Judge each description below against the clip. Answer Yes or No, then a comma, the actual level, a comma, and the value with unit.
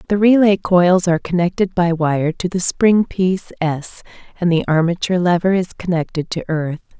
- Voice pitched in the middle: Yes, medium, 175 Hz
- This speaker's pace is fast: No, average, 170 wpm